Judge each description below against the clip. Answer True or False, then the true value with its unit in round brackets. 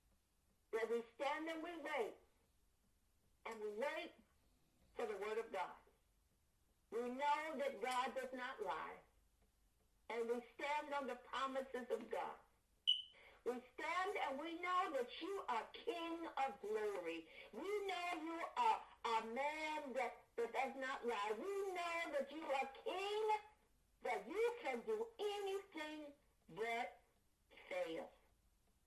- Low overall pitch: False (300 Hz)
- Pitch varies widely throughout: True (8.1 semitones)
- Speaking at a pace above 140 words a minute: False (135 wpm)